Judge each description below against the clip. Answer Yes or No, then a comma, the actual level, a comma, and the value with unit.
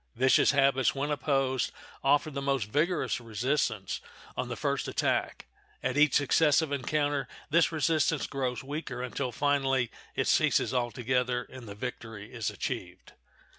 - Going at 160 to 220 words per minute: No, slow, 135 wpm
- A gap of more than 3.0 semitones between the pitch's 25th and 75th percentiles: No, average, 2.7 semitones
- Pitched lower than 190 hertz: Yes, low, 135 Hz